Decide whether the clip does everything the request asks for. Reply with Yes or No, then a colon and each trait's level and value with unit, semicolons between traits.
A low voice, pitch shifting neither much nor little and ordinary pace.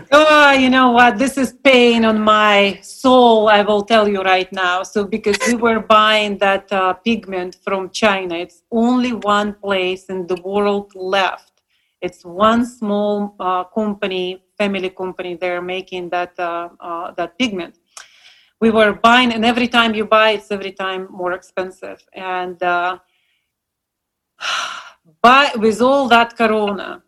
No: high, 205 Hz; average, 3.6 semitones; average, 150 wpm